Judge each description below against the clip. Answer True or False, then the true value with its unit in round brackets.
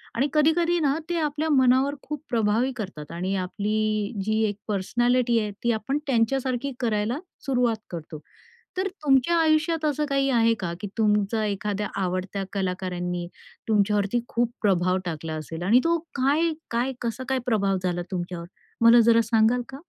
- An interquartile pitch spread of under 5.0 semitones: False (5.3 semitones)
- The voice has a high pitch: True (225 Hz)